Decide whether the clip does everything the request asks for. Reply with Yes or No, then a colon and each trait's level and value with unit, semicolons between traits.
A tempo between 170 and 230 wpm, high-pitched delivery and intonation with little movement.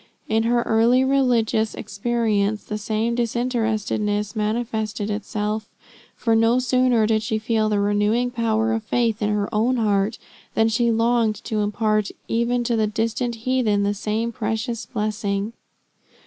No: average, 145 wpm; high, 220 Hz; narrow, 1.8 semitones